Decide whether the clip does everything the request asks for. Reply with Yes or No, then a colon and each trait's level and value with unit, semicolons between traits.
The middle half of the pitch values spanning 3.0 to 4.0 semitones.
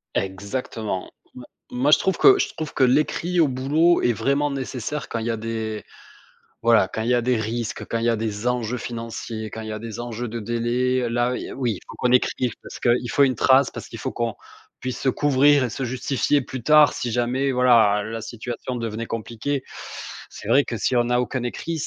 No: narrow, 2.5 semitones